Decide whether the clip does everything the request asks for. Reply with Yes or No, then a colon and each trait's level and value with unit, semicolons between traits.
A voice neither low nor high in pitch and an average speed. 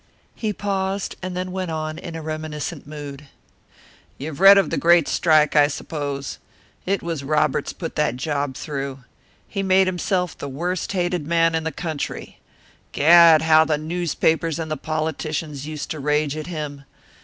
Yes: medium, 155 Hz; average, 165 wpm